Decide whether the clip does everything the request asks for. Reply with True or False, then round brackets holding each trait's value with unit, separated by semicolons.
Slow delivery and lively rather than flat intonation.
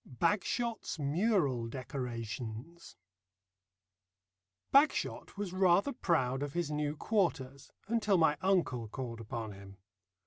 True (100 wpm; 7.2 semitones)